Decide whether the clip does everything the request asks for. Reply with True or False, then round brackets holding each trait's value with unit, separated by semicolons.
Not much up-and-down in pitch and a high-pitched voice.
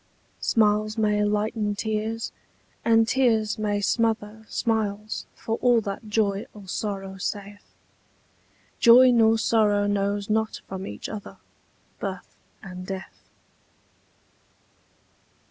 True (1.6 semitones; 210 Hz)